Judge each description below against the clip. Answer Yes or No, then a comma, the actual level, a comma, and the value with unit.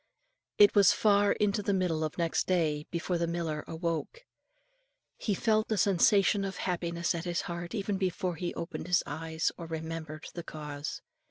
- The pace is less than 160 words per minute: No, average, 170 wpm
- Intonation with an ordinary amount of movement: Yes, average, 3.3 semitones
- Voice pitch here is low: No, medium, 170 Hz